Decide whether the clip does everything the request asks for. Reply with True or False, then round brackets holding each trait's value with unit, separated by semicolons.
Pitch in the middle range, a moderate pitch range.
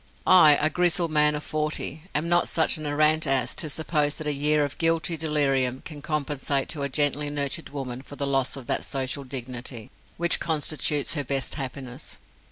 False (145 Hz; 2.2 semitones)